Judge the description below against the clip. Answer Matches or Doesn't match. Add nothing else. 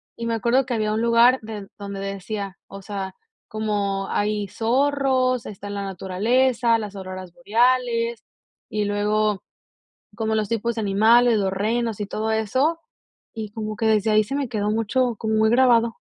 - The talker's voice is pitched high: Matches